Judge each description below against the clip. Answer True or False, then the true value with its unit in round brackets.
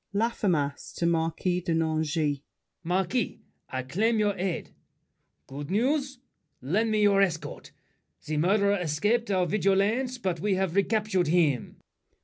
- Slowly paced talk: True (125 wpm)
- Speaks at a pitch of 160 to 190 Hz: True (185 Hz)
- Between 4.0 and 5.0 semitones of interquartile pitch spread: True (4.6 semitones)